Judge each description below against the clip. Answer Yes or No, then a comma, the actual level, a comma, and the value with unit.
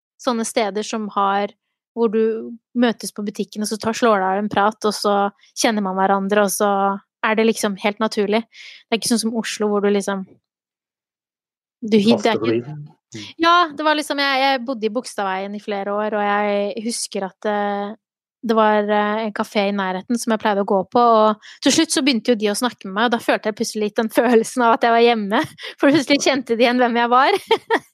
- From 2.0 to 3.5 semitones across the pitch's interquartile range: Yes, average, 2.9 semitones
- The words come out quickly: Yes, fast, 215 wpm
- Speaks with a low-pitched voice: No, high, 220 Hz